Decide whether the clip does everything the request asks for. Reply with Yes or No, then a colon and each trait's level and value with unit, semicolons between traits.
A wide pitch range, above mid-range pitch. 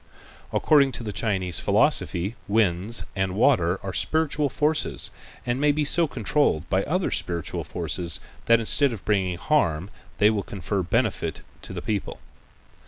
No: wide, 7.2 semitones; low, 105 Hz